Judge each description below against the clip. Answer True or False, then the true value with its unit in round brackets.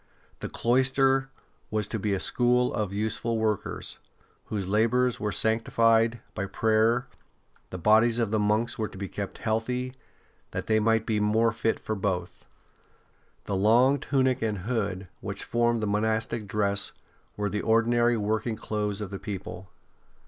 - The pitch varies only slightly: True (2.2 semitones)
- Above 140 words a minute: True (155 wpm)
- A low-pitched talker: True (110 Hz)